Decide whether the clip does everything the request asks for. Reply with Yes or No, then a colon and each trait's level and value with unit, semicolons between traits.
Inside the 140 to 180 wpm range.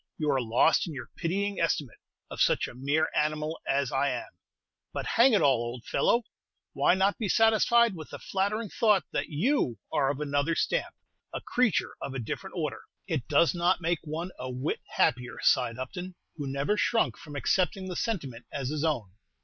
No: average, 190 wpm